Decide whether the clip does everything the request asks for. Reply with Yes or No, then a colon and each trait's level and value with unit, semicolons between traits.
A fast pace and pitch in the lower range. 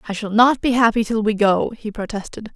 No: fast, 235 wpm; high, 220 Hz